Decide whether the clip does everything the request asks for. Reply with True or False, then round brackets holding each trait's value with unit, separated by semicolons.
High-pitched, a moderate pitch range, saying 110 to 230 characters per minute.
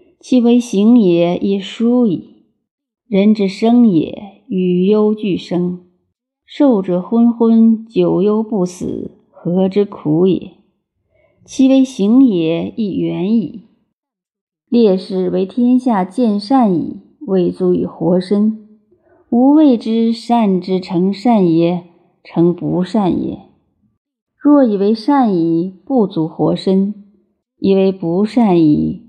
True (200 Hz; 4.6 semitones; 150 characters per minute)